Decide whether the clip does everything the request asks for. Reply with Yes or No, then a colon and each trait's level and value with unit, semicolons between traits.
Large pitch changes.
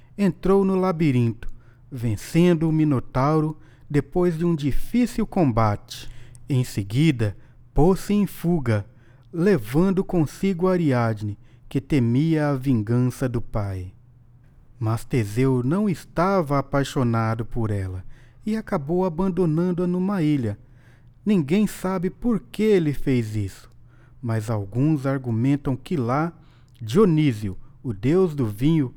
Yes: wide, 6.2 semitones